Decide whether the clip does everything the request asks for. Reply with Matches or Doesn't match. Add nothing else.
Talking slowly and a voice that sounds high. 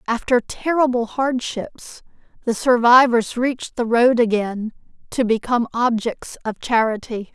Matches